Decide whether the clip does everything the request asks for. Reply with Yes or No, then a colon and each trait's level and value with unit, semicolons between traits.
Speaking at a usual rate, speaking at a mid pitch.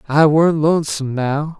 Yes: average, 150 wpm; medium, 150 Hz